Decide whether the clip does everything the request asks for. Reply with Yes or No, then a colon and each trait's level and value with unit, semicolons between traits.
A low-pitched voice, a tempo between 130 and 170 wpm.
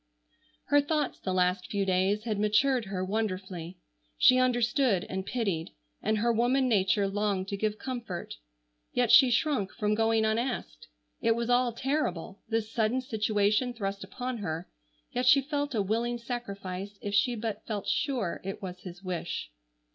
No: high, 215 Hz; average, 160 wpm